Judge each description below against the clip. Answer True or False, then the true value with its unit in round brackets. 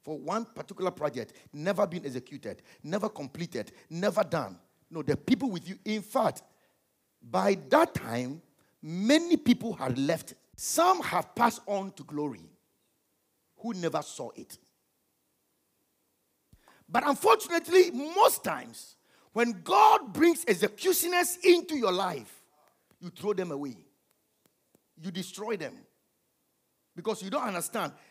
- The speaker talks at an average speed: False (120 wpm)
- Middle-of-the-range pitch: False (205 Hz)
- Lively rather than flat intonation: True (8.3 semitones)